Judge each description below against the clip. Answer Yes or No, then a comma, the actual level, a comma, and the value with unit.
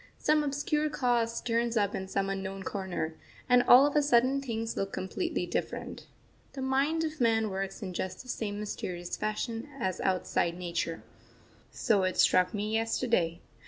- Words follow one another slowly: No, average, 160 wpm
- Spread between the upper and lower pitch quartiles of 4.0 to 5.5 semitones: Yes, average, 5.0 semitones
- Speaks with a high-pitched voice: Yes, high, 225 Hz